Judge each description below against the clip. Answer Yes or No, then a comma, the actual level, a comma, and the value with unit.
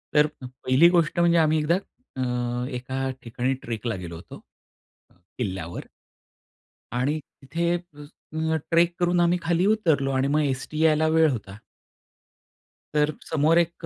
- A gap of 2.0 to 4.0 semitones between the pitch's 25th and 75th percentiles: No, average, 4.6 semitones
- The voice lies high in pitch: No, medium, 150 Hz